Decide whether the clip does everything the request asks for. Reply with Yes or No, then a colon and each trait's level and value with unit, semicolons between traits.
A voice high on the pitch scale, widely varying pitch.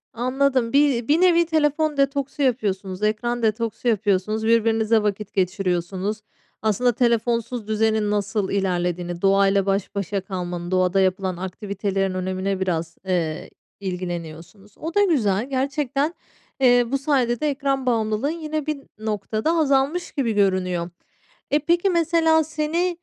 Yes: high, 220 Hz; wide, 6.3 semitones